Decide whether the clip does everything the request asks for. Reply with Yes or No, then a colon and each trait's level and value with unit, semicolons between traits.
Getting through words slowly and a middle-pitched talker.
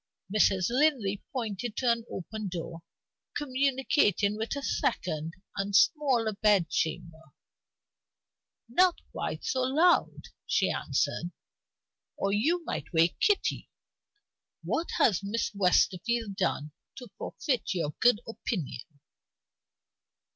No: slow, 105 wpm; high, 215 Hz